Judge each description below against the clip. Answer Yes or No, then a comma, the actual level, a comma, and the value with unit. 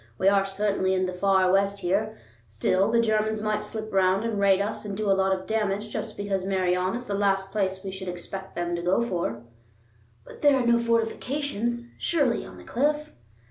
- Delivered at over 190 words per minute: Yes, fast, 205 wpm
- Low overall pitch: No, high, 200 Hz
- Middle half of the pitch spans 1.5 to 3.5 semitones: Yes, average, 2.7 semitones